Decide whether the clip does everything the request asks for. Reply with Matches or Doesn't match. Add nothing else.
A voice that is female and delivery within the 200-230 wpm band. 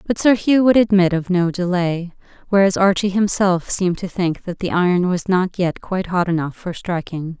Matches